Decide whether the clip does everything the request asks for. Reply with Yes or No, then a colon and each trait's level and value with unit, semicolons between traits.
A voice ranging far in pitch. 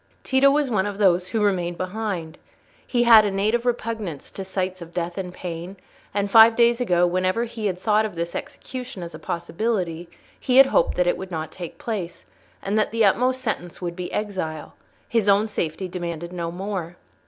No: average, 4.1 semitones